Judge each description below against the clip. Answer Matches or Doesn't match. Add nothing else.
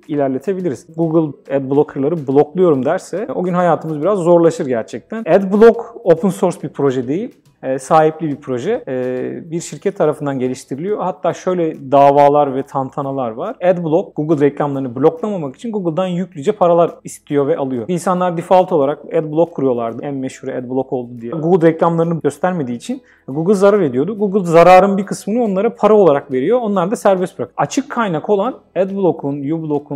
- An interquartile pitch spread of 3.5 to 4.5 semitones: Doesn't match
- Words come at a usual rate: Doesn't match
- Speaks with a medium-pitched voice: Matches